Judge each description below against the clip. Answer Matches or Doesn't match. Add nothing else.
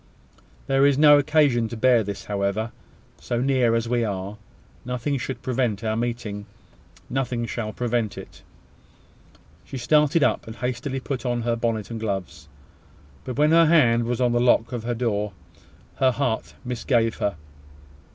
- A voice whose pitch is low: Matches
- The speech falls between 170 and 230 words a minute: Doesn't match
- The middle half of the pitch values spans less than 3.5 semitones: Matches